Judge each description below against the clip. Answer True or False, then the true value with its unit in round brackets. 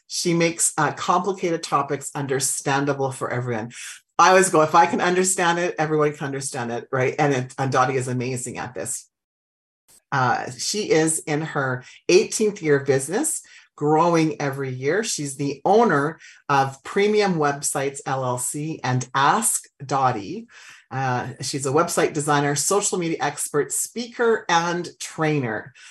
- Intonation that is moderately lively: True (4.4 semitones)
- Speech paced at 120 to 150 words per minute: True (145 wpm)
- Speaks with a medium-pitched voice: True (145 Hz)